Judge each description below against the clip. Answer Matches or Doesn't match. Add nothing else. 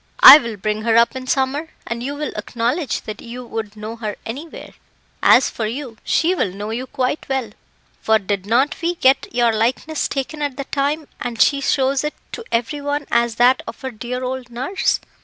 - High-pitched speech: Matches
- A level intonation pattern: Doesn't match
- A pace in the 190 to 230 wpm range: Matches